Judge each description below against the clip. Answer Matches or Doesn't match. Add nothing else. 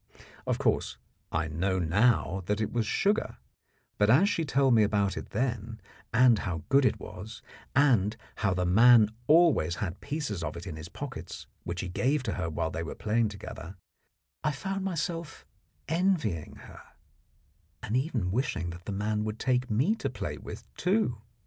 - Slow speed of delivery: Doesn't match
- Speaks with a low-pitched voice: Matches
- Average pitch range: Doesn't match